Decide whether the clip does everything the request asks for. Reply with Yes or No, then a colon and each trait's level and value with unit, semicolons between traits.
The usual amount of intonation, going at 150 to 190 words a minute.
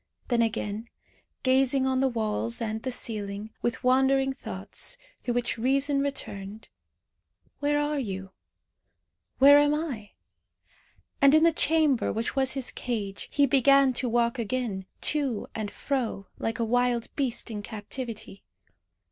No: average, 3.8 semitones; average, 140 wpm